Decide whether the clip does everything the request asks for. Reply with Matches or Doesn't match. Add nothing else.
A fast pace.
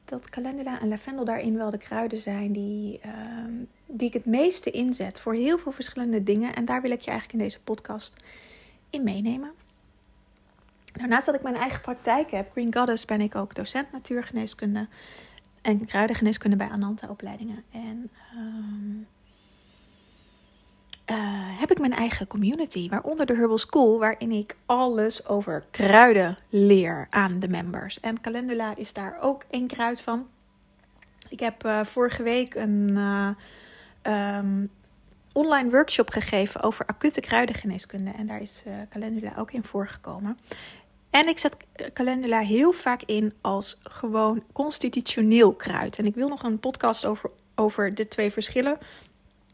Doesn't match